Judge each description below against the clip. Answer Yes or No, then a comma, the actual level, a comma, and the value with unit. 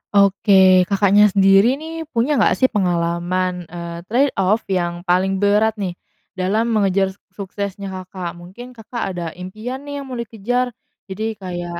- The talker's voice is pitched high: Yes, high, 195 Hz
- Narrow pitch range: No, average, 3.3 semitones